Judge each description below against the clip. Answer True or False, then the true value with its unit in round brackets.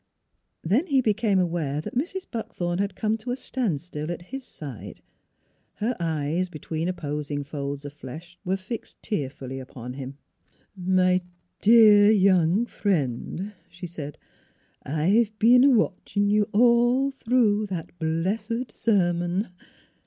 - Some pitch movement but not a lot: False (5.8 semitones)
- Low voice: False (185 Hz)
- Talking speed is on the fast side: False (145 wpm)